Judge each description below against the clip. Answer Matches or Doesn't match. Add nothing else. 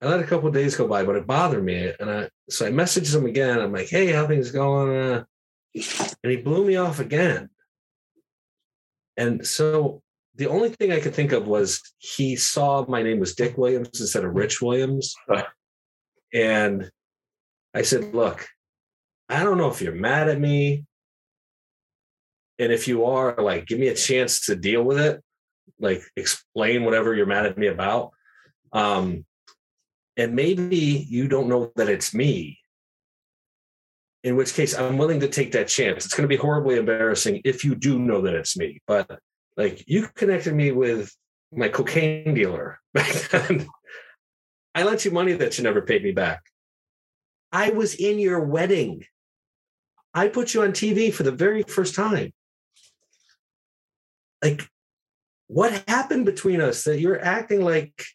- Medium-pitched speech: Matches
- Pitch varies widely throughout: Matches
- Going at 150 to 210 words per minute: Matches